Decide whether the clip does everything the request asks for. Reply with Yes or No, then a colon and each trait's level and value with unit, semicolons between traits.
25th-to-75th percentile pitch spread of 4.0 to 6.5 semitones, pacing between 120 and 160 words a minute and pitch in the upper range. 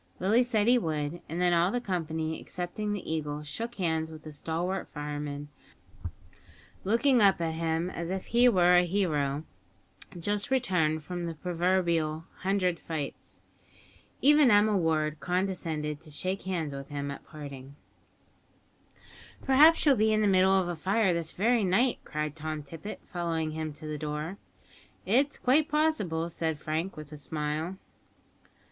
No: average, 4.4 semitones; average, 155 wpm; medium, 170 Hz